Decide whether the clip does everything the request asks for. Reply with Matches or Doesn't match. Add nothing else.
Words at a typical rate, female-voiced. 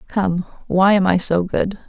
Matches